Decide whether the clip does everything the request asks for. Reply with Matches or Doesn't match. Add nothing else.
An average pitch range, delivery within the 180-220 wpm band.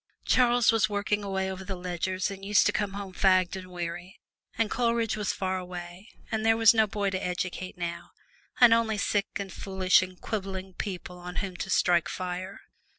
Doesn't match